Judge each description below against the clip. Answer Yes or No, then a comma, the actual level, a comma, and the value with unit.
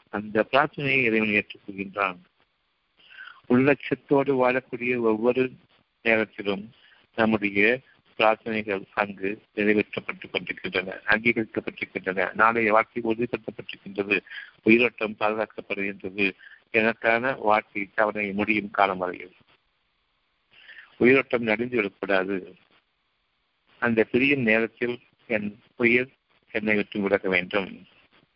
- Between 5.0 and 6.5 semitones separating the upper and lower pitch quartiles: No, average, 2.9 semitones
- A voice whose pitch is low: Yes, low, 110 Hz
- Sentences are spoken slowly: Yes, slow, 60 wpm